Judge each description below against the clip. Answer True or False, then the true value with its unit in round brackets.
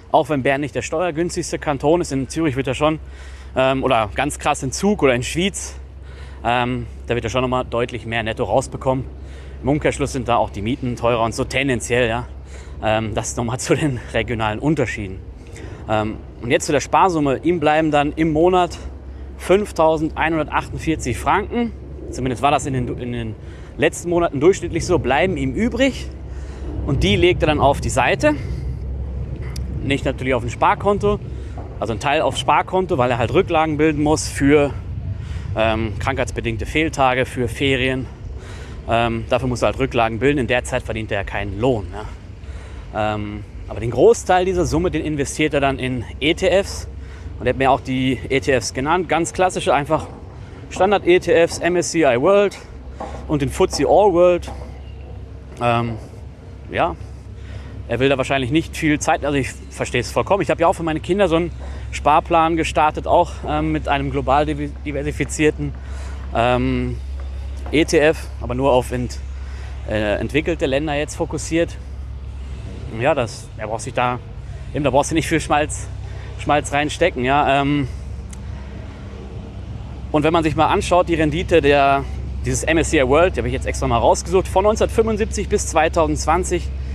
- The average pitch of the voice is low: True (125 Hz)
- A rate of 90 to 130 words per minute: False (160 wpm)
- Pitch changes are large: True (7.6 semitones)